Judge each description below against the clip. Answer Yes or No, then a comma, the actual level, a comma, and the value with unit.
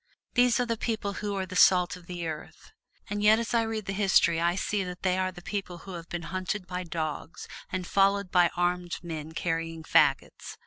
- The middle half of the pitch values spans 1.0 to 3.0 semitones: Yes, average, 2.7 semitones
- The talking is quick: Yes, fast, 210 wpm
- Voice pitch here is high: No, medium, 180 Hz